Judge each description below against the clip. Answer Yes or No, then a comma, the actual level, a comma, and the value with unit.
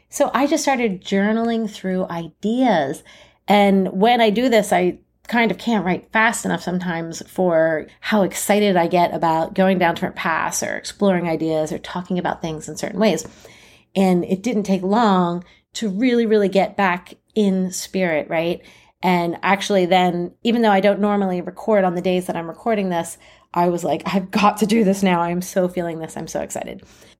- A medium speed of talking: Yes, average, 190 wpm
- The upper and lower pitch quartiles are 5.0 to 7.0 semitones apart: No, average, 3.3 semitones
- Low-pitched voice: No, high, 190 Hz